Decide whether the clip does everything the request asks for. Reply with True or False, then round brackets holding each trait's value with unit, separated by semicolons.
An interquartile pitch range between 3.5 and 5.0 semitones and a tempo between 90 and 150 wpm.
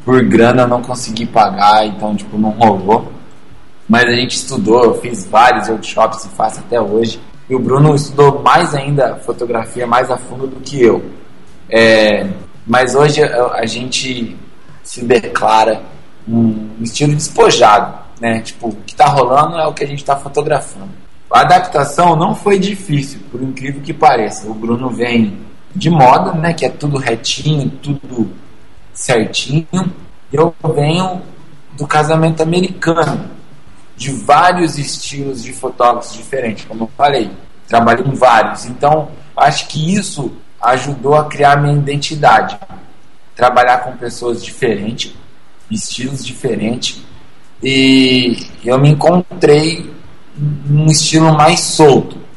True (4.1 semitones; 135 wpm)